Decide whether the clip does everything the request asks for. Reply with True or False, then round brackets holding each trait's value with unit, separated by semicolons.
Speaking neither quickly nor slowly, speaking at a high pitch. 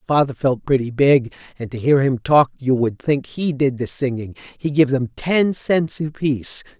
False (195 wpm; 135 Hz)